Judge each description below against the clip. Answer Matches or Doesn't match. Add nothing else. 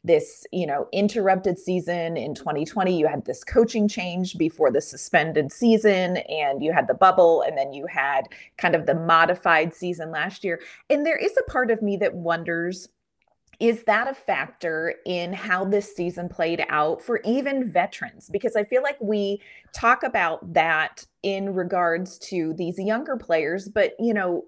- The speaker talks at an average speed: Matches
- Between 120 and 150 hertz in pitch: Doesn't match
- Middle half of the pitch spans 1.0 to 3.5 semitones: Doesn't match